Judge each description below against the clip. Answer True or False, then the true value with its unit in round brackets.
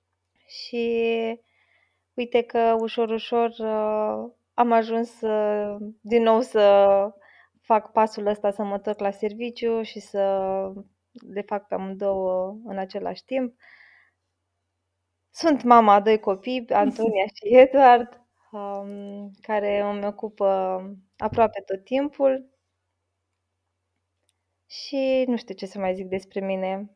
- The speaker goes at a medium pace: False (110 wpm)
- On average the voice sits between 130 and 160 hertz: False (210 Hz)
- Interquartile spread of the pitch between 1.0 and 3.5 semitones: True (3.1 semitones)